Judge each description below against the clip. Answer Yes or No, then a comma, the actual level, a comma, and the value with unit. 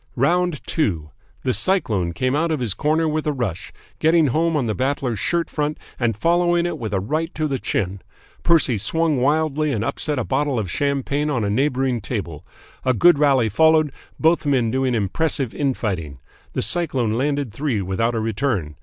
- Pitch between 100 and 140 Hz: Yes, low, 135 Hz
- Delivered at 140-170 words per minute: No, average, 190 wpm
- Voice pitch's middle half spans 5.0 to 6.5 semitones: Yes, wide, 5.6 semitones